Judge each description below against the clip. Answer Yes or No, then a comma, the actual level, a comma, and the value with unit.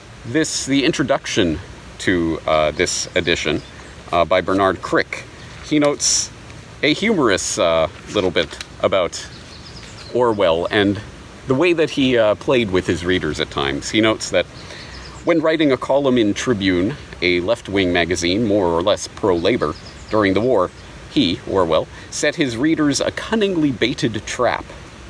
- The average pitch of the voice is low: Yes, low, 105 Hz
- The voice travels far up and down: Yes, wide, 8.0 semitones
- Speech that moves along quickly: No, average, 145 wpm